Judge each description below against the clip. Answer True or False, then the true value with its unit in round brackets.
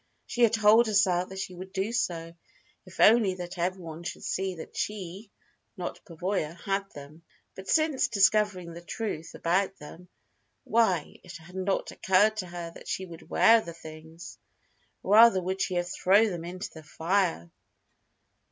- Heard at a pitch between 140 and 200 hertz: True (185 Hz)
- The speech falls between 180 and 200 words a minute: False (160 wpm)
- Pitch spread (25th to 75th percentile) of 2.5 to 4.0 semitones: True (3.2 semitones)